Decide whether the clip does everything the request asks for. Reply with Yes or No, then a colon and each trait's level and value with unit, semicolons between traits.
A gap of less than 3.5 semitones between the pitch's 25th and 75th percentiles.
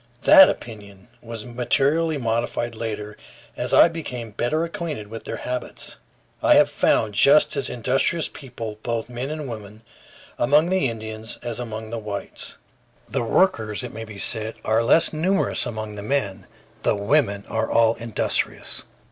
No: average, 4.1 semitones